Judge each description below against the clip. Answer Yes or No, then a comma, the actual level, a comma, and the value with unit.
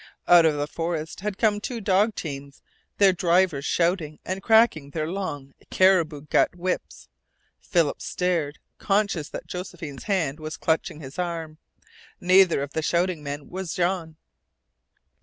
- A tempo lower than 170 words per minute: Yes, average, 140 wpm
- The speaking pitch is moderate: Yes, medium, 170 Hz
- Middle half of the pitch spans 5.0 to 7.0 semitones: No, average, 3.7 semitones